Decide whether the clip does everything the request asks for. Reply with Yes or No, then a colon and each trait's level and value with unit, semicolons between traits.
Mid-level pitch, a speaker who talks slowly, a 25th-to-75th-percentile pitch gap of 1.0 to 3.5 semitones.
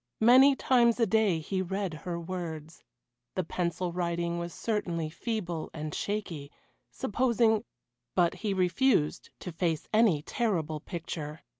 No: medium, 180 Hz; slow, 130 wpm; average, 4.8 semitones